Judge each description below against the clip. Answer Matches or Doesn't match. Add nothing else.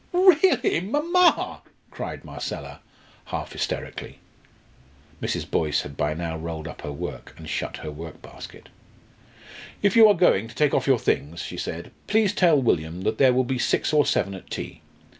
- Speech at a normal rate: Matches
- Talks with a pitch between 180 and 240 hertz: Doesn't match